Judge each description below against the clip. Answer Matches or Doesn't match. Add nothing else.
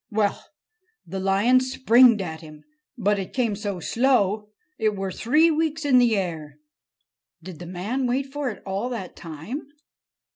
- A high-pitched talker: Matches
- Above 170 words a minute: Doesn't match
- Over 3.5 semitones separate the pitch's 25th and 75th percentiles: Matches